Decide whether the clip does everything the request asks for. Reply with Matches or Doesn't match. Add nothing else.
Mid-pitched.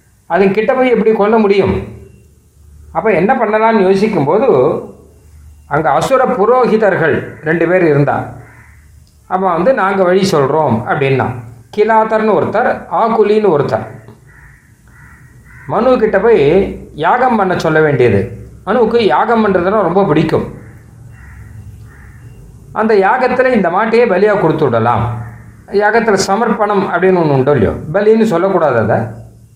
Matches